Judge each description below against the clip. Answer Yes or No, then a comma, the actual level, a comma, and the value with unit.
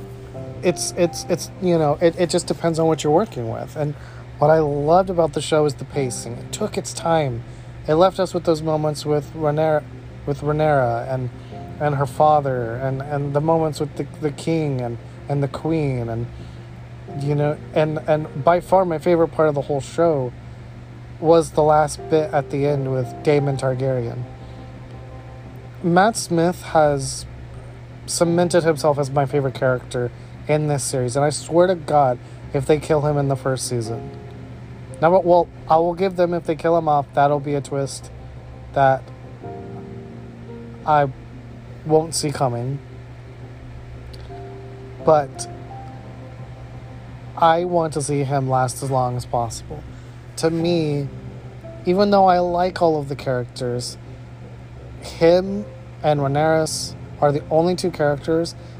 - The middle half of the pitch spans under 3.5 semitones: No, average, 4.1 semitones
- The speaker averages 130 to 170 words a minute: Yes, average, 155 wpm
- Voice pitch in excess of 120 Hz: Yes, medium, 140 Hz